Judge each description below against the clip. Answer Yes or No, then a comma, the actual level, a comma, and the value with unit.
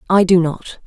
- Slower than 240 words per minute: Yes, fast, 210 wpm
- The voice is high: No, medium, 175 Hz